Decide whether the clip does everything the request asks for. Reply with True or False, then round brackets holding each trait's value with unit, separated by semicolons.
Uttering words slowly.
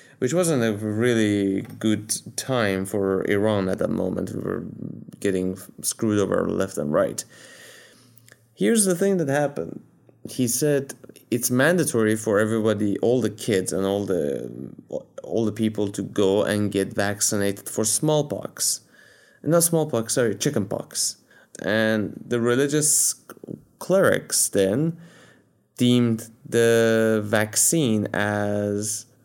True (120 wpm)